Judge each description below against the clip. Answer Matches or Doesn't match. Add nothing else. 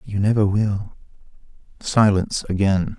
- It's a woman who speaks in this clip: Doesn't match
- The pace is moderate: Doesn't match